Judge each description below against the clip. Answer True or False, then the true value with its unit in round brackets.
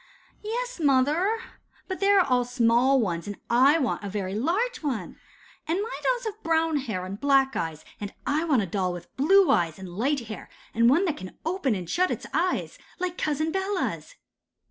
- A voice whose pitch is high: True (280 Hz)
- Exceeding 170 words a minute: True (190 wpm)